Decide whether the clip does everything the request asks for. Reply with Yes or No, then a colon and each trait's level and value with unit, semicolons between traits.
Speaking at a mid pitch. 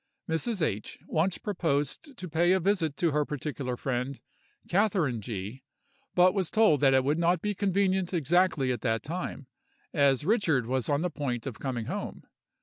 Yes: medium, 155 Hz